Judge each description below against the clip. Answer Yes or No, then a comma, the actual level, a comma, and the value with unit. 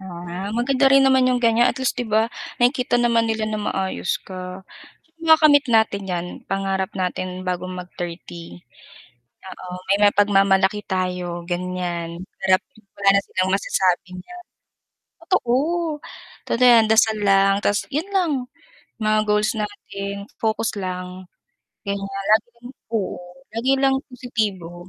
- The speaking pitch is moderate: No, high, 200 Hz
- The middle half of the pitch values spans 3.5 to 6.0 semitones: Yes, average, 4.3 semitones